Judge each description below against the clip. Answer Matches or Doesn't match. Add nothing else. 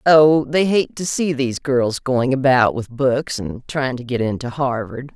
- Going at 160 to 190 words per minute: Doesn't match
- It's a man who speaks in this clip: Doesn't match